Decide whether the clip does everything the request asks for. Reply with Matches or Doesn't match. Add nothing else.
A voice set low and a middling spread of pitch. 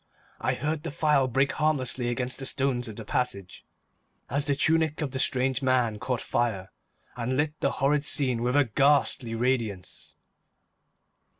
Matches